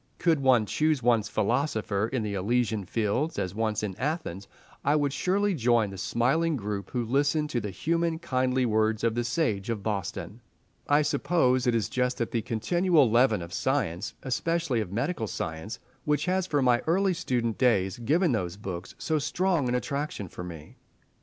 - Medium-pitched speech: No, low, 125 Hz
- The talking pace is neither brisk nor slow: Yes, average, 175 wpm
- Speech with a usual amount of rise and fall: No, wide, 5.8 semitones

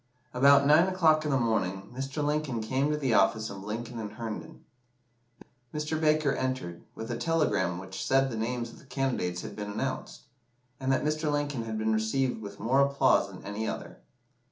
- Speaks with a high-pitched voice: No, low, 130 Hz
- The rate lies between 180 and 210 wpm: Yes, average, 185 wpm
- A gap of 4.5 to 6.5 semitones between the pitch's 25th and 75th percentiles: Yes, average, 5.0 semitones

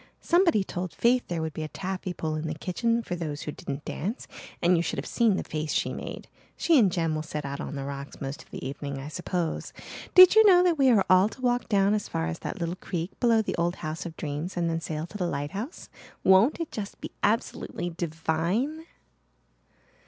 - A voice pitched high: No, medium, 175 Hz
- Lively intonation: Yes, wide, 6.0 semitones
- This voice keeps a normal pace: No, fast, 225 wpm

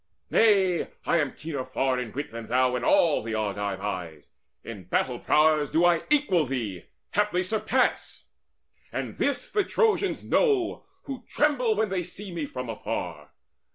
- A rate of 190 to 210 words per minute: No, average, 155 wpm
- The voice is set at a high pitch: No, medium, 155 Hz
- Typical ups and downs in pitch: No, wide, 9.0 semitones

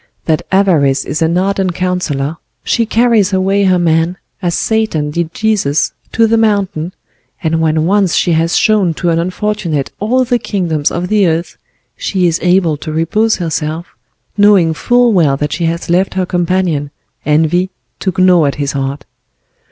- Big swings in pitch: No, average, 3.7 semitones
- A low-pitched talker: No, medium, 175 Hz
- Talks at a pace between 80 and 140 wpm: No, average, 165 wpm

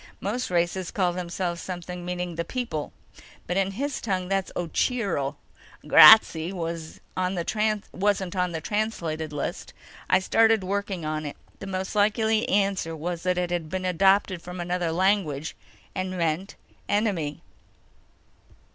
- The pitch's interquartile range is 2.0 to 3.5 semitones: Yes, average, 2.8 semitones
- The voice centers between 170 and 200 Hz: Yes, medium, 185 Hz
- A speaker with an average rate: No, slow, 130 wpm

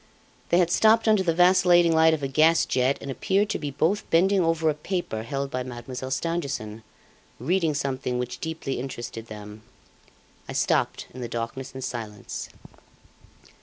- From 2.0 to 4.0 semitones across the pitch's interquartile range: No, wide, 5.4 semitones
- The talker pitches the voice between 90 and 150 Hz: Yes, medium, 140 Hz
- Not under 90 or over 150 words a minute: No, average, 165 wpm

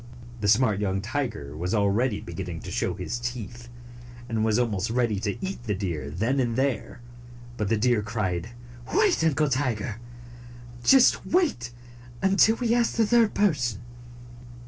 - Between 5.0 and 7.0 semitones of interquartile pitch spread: Yes, average, 5.3 semitones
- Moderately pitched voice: No, low, 120 Hz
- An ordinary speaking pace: Yes, average, 150 wpm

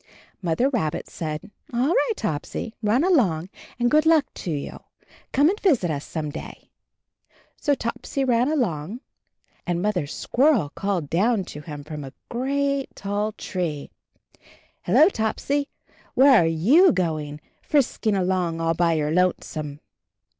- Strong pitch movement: Yes, wide, 8.7 semitones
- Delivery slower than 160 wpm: Yes, average, 140 wpm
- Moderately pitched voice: No, high, 200 Hz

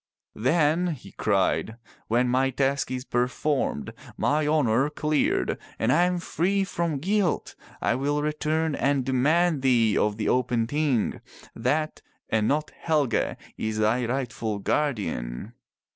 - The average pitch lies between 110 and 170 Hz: Yes, low, 135 Hz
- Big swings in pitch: No, average, 4.8 semitones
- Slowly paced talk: Yes, slow, 130 wpm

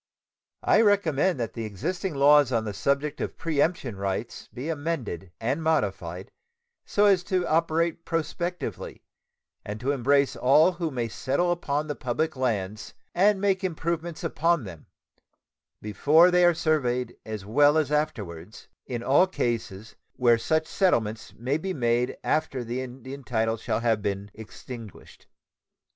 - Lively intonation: Yes, wide, 6.3 semitones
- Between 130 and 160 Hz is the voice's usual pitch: Yes, medium, 140 Hz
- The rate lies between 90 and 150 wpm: Yes, average, 145 wpm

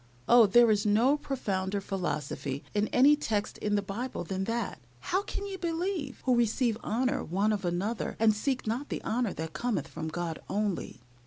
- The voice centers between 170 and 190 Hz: No, high, 215 Hz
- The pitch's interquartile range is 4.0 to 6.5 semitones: Yes, average, 4.8 semitones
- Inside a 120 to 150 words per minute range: No, average, 180 wpm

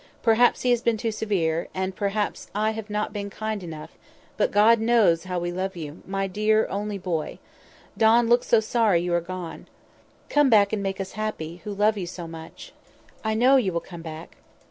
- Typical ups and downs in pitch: Yes, average, 3.8 semitones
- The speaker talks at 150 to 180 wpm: No, average, 200 wpm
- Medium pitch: No, high, 200 Hz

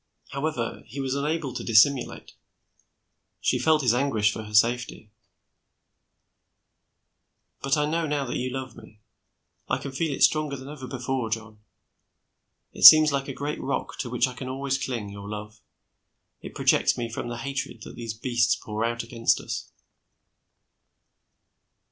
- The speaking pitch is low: Yes, low, 130 Hz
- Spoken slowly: No, average, 155 wpm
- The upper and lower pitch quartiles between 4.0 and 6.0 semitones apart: No, average, 3.3 semitones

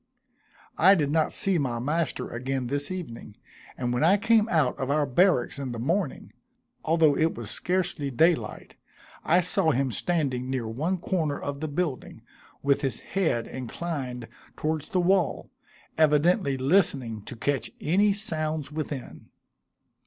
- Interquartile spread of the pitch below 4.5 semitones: No, average, 4.9 semitones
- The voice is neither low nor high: Yes, medium, 150 Hz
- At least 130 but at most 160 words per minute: Yes, average, 145 wpm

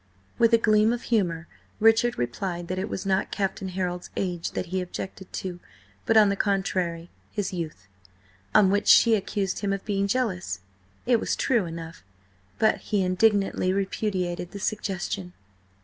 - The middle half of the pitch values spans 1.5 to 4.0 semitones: Yes, average, 2.9 semitones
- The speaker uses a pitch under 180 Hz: No, high, 190 Hz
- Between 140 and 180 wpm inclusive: Yes, average, 160 wpm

